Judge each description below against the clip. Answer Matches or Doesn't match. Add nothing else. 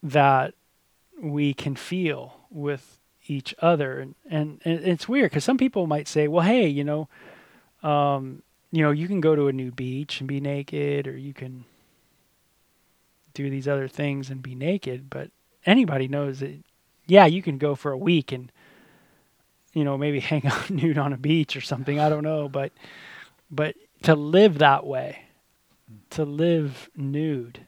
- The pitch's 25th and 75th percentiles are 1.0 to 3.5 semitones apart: Matches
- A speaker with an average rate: Matches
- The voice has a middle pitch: Matches